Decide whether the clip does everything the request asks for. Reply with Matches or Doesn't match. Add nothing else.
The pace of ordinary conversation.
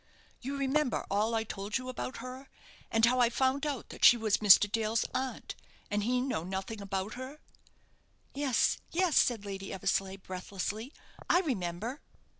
Matches